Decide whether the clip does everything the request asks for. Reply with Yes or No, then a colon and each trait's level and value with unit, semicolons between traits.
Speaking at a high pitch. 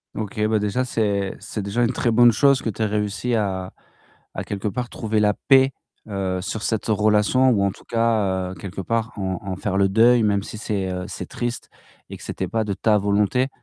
No: low, 105 Hz